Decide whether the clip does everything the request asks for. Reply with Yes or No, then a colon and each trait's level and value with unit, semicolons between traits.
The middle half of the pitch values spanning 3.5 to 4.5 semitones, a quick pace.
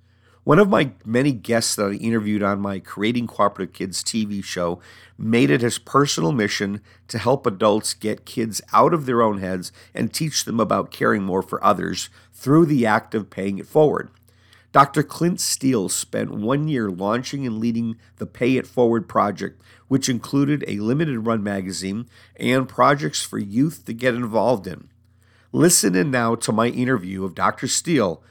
No: average, 4.0 semitones; average, 175 wpm